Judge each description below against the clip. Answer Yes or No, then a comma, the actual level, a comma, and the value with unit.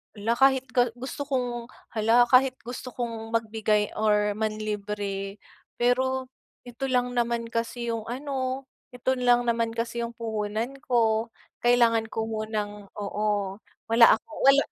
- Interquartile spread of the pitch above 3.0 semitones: No, narrow, 2.4 semitones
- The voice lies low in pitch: No, high, 230 Hz